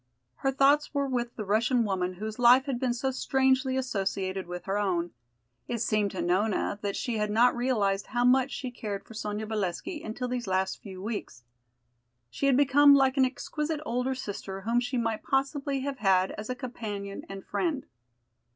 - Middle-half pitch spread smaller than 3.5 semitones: No, average, 4.7 semitones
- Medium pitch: No, high, 235 Hz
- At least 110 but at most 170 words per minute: No, average, 185 wpm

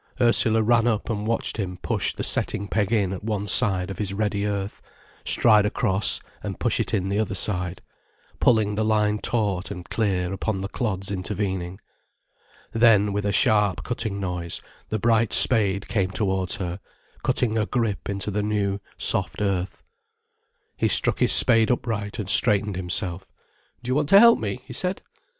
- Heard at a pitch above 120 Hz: No, low, 105 Hz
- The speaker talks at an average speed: Yes, average, 170 wpm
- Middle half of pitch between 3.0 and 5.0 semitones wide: No, narrow, 2.4 semitones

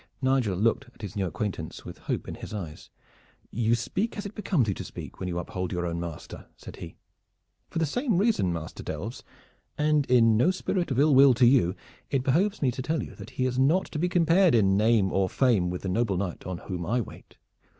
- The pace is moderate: No, fast, 225 wpm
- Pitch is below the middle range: Yes, low, 120 Hz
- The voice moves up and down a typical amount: No, wide, 8.2 semitones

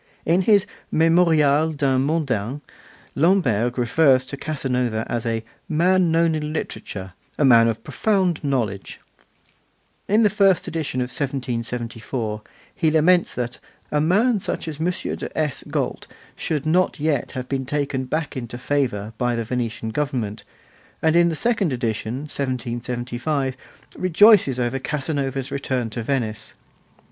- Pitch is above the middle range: No, medium, 140 Hz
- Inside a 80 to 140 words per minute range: Yes, slow, 135 wpm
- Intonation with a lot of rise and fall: No, average, 4.8 semitones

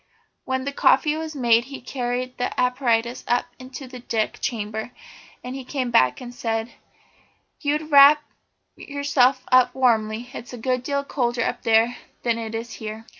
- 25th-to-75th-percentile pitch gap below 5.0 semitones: Yes, narrow, 2.6 semitones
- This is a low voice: No, very high, 250 Hz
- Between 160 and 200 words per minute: Yes, average, 170 wpm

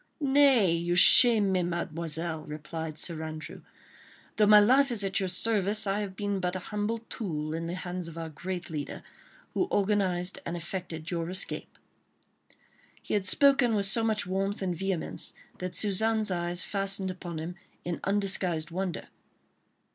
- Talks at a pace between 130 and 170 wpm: Yes, average, 160 wpm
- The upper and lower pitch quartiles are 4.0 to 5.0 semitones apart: No, average, 3.3 semitones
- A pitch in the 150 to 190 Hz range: Yes, medium, 185 Hz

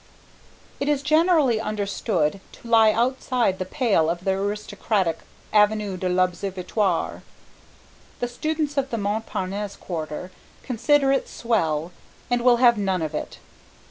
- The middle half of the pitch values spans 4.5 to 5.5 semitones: Yes, average, 4.8 semitones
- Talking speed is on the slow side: Yes, slow, 130 wpm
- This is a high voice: Yes, high, 210 Hz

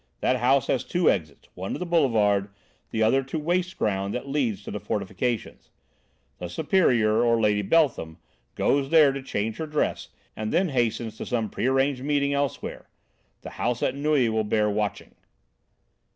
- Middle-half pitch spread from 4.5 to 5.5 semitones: Yes, average, 4.9 semitones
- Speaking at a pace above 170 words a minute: No, average, 165 wpm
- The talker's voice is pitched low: Yes, low, 125 Hz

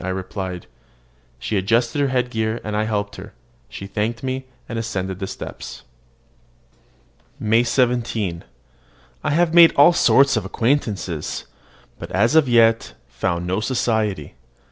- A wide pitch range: No, average, 4.3 semitones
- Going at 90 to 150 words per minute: Yes, average, 140 wpm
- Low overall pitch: Yes, low, 115 Hz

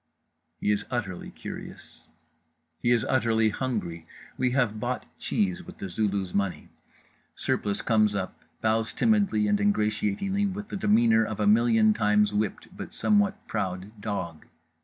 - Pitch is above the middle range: No, low, 110 Hz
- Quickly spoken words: No, average, 140 wpm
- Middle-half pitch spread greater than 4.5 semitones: No, average, 3.4 semitones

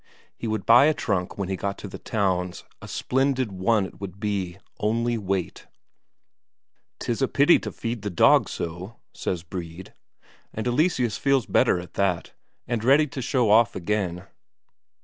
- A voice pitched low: Yes, low, 105 Hz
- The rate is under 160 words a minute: No, average, 165 wpm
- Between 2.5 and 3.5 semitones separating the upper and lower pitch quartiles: No, average, 4.3 semitones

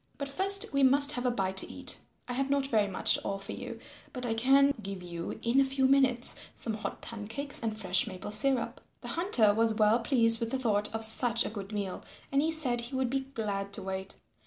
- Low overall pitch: No, high, 235 Hz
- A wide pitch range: No, average, 4.6 semitones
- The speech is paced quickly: Yes, fast, 230 wpm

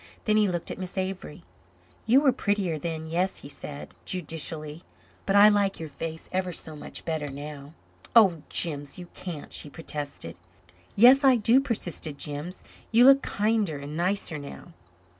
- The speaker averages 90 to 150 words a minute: No, average, 160 wpm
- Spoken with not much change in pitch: No, average, 5.2 semitones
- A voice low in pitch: No, medium, 175 Hz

